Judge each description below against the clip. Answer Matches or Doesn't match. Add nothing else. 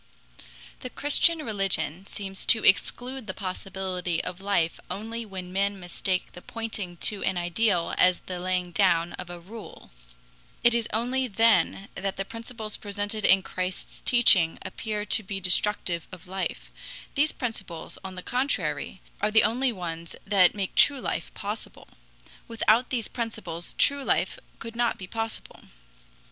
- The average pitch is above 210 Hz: Doesn't match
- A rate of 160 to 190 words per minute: Doesn't match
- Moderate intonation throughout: Matches